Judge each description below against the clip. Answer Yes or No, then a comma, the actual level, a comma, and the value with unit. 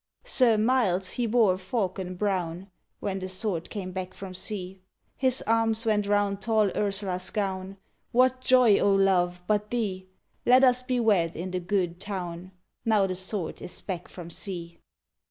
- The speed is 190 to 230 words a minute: No, average, 170 wpm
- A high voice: Yes, high, 195 Hz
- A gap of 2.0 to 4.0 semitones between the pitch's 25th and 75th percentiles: Yes, average, 3.2 semitones